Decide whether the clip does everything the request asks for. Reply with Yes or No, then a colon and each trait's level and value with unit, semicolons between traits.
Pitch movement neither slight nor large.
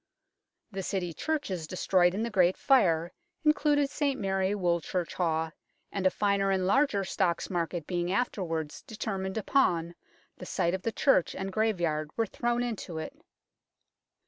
Yes: average, 4.2 semitones